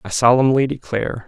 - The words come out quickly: No, average, 140 wpm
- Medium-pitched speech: No, low, 120 Hz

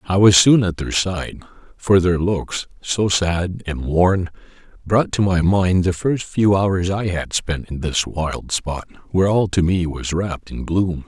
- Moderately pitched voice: No, very low, 90 Hz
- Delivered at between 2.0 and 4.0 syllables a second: Yes, 3.9 syllables/s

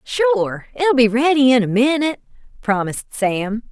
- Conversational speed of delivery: Yes, average, 145 wpm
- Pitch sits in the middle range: No, very high, 250 Hz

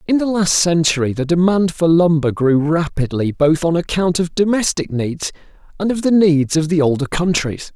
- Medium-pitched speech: Yes, medium, 165 Hz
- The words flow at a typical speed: Yes, average, 185 wpm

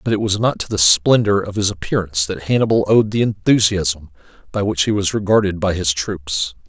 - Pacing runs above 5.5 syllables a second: No, 5.4 syllables/s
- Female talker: No, male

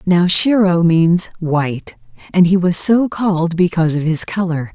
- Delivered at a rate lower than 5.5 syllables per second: Yes, 4.6 syllables/s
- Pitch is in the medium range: Yes, medium, 175 Hz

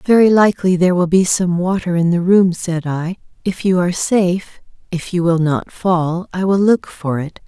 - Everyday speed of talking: No, fast, 210 wpm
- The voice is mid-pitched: Yes, medium, 180 Hz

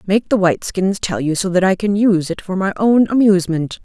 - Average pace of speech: No, fast, 235 wpm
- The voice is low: No, high, 190 Hz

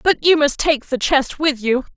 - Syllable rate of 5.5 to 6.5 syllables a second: No, 4.4 syllables/s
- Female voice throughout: Yes, female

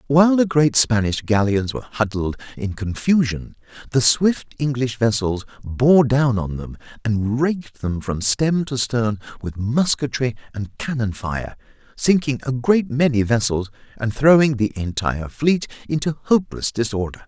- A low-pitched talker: Yes, low, 125 Hz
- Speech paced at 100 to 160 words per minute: Yes, average, 145 wpm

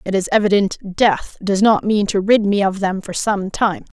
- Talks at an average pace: No, fast, 225 wpm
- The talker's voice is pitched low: No, high, 200 Hz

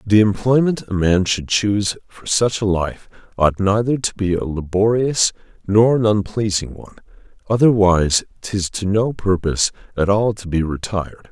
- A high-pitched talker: No, low, 100 Hz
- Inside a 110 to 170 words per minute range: Yes, average, 160 wpm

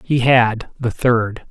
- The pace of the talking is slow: Yes, slow, 120 wpm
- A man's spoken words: Yes, male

